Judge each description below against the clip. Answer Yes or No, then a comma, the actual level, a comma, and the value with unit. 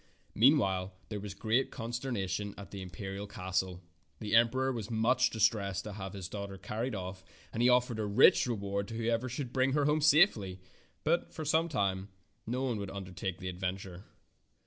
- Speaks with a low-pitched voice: Yes, low, 105 Hz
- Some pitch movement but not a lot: Yes, average, 4.3 semitones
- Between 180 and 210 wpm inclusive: Yes, average, 190 wpm